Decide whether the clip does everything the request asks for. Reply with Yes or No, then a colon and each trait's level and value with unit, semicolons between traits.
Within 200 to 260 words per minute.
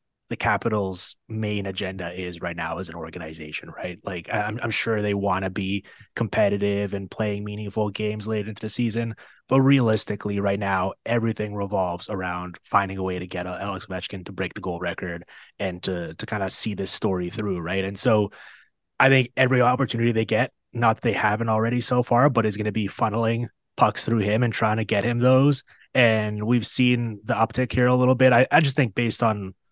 Yes: fast, 205 wpm